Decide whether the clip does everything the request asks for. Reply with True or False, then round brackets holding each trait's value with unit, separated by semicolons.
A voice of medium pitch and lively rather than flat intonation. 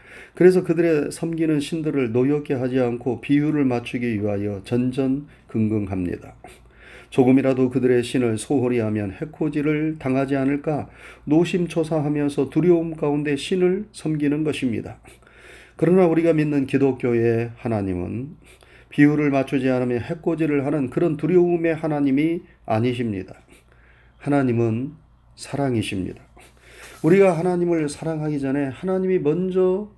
False (145 Hz; 4.6 semitones)